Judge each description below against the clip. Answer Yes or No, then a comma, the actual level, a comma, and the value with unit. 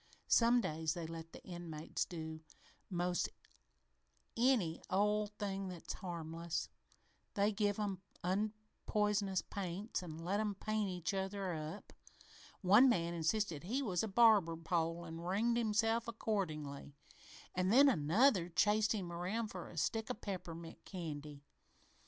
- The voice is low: No, high, 190 Hz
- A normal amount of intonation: Yes, average, 4.2 semitones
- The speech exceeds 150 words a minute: No, slow, 135 wpm